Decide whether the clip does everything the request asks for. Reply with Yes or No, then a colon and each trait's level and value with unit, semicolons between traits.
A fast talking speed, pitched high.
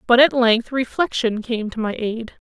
No: average, 195 wpm; high, 235 Hz